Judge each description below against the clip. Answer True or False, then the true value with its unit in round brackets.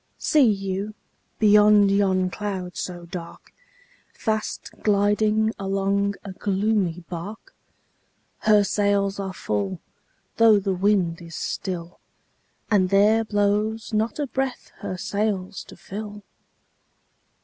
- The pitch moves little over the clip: True (2.2 semitones)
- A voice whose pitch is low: False (200 Hz)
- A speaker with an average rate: False (110 wpm)